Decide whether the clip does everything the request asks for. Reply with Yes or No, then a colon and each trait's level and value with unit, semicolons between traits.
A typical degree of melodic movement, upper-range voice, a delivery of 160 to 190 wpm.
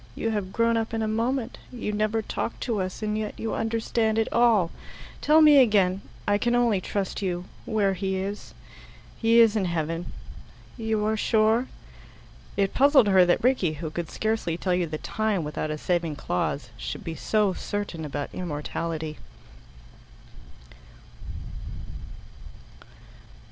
No: average, 4.2 semitones; high, 205 Hz; average, 150 wpm